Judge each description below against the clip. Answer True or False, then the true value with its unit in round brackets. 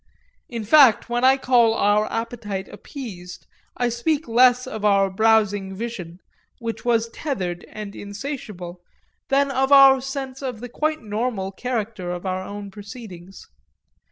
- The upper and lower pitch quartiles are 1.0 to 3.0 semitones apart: False (4.2 semitones)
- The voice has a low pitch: False (225 Hz)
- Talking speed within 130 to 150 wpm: True (140 wpm)